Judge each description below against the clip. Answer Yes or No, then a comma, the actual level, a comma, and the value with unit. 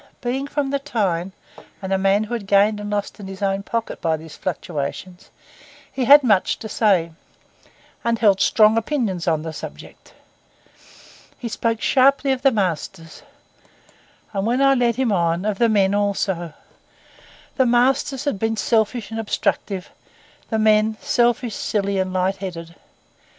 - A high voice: Yes, high, 210 Hz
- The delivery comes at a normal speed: Yes, average, 155 wpm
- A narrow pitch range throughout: No, average, 3.9 semitones